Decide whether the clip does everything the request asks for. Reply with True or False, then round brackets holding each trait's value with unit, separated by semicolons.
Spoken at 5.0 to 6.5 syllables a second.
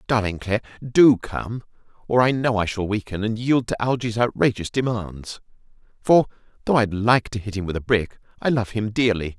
True (5.3 syllables/s)